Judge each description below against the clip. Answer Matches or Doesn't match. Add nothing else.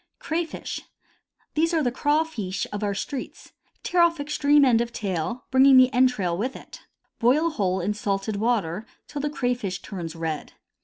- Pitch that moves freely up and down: Matches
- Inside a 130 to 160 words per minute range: Doesn't match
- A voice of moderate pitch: Doesn't match